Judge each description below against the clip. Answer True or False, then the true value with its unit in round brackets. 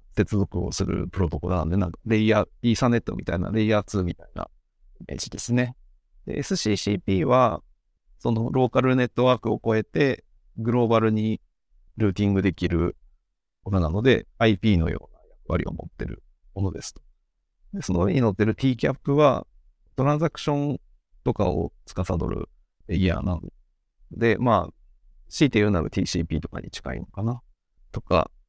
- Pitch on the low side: True (105 Hz)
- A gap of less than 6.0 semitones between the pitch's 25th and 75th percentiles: True (5.2 semitones)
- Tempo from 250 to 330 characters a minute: False (340 characters per minute)